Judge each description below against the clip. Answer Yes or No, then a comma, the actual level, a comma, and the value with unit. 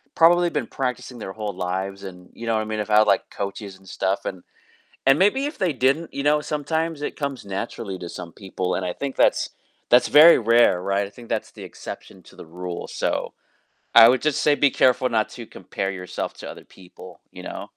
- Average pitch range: No, wide, 6.9 semitones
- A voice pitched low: Yes, low, 115 Hz